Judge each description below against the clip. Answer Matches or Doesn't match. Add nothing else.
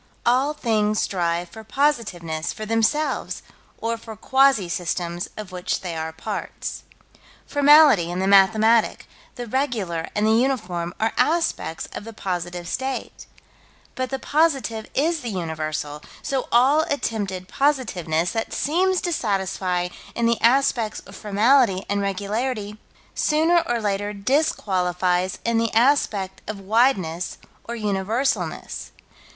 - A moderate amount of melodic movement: Doesn't match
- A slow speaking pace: Matches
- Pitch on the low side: Doesn't match